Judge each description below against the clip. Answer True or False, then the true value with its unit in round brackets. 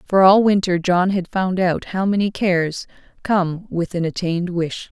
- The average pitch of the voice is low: False (185 Hz)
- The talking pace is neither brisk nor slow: True (180 wpm)